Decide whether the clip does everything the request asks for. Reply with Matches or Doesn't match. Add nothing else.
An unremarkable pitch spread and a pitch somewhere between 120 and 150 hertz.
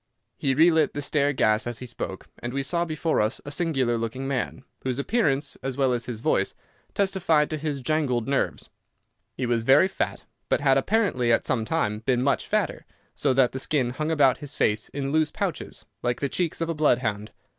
Matches